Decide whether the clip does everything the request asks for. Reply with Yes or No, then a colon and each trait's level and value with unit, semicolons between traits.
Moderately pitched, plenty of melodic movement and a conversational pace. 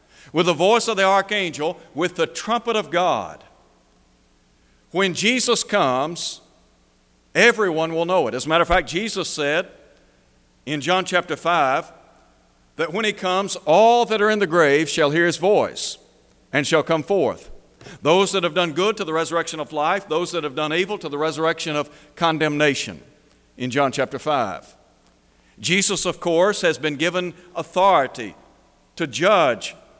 No: medium, 165 Hz; average, 4.6 semitones; average, 160 wpm